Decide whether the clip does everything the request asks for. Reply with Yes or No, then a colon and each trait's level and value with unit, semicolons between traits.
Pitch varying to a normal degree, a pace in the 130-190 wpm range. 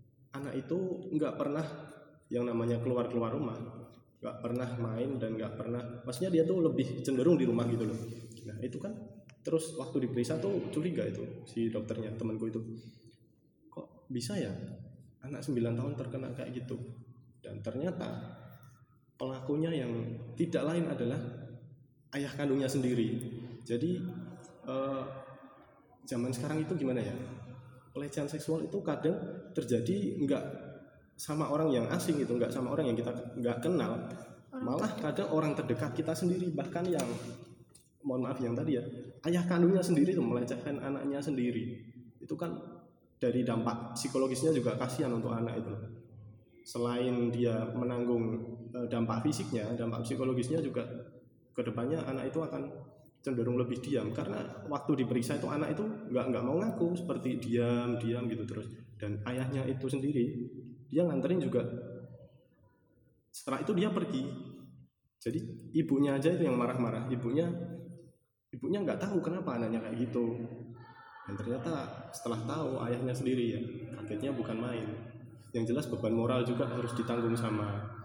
Yes: average, 3.2 semitones; fast, 140 wpm